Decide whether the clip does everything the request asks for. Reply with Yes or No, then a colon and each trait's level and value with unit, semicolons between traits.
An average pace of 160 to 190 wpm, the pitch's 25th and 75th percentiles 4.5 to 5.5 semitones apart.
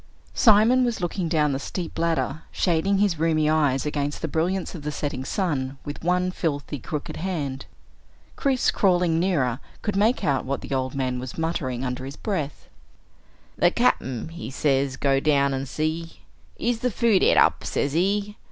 Yes: average, 170 wpm; average, 5.0 semitones